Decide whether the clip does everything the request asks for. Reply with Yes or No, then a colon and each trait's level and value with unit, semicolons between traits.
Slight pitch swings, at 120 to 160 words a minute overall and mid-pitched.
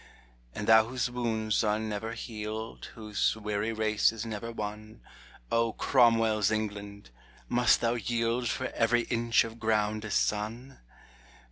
No: narrow, 1.5 semitones; slow, 135 wpm; low, 110 Hz